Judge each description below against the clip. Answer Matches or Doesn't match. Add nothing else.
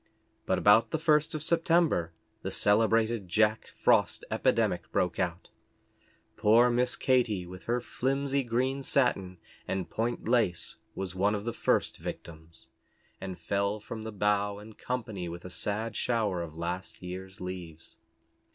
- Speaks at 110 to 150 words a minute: Matches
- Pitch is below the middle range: Matches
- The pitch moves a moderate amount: Matches